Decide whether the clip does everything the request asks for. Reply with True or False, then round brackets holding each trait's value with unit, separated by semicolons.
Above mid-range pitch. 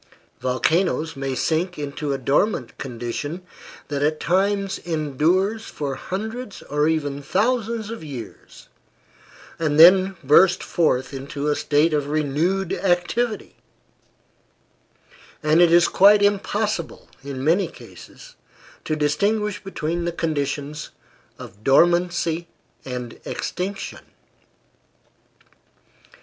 False (165 Hz)